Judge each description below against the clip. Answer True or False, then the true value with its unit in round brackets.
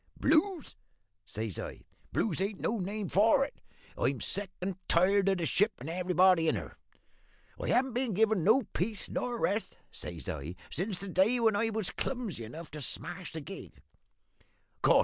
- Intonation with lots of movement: False (4.6 semitones)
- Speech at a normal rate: True (170 wpm)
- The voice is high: True (195 Hz)